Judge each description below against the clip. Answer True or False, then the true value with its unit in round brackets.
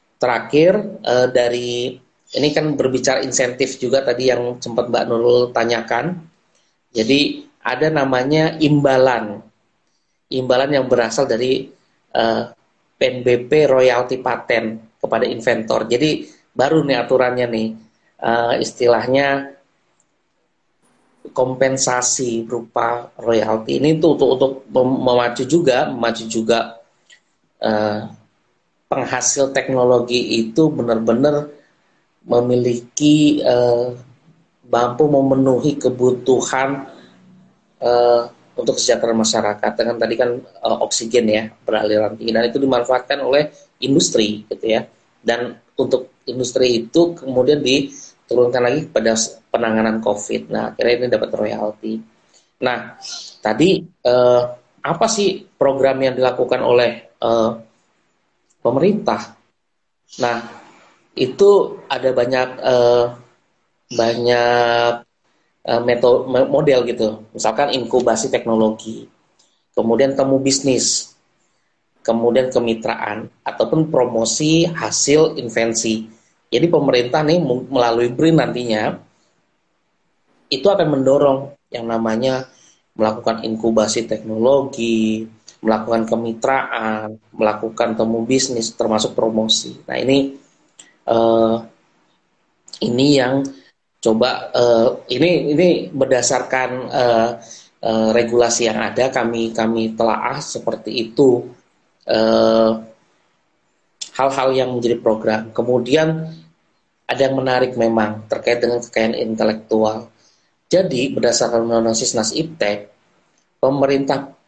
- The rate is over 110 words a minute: False (95 wpm)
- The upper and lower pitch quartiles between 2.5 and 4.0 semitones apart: True (3.0 semitones)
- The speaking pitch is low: True (120 Hz)